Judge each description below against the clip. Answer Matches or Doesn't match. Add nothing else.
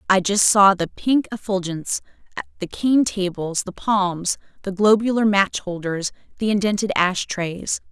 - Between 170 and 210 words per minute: Doesn't match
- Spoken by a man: Doesn't match